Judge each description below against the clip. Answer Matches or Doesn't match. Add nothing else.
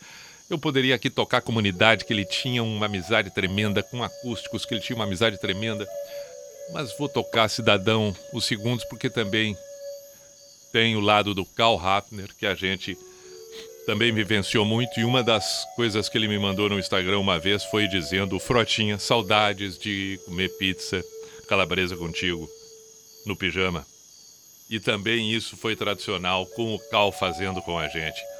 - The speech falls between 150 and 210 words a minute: Matches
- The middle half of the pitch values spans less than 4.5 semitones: Matches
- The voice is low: Matches